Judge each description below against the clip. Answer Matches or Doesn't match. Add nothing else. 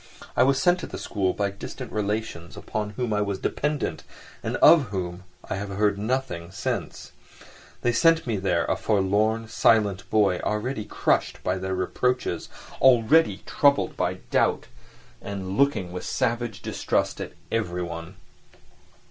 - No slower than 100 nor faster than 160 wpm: Matches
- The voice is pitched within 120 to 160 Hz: Doesn't match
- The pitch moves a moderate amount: Matches